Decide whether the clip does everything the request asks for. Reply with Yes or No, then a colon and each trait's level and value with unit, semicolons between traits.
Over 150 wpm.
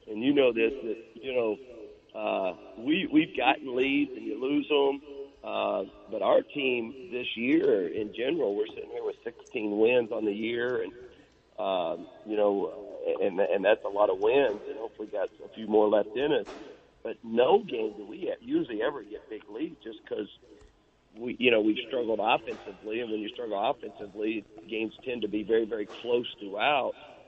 Yes: average, 190 wpm